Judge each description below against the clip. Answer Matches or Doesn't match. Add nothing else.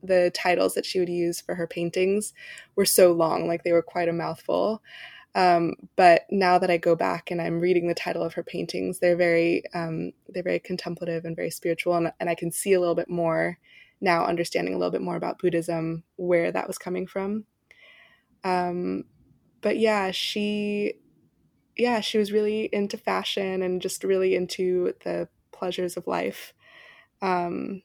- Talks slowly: Doesn't match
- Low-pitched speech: Doesn't match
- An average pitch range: Doesn't match